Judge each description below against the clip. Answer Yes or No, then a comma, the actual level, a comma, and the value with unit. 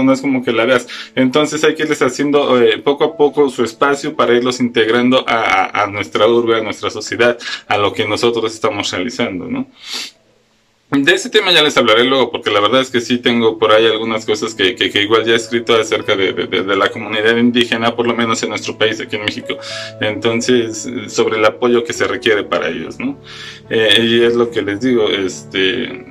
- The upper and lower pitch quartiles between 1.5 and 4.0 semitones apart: Yes, average, 2.8 semitones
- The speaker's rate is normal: No, fast, 220 wpm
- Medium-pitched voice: No, low, 120 Hz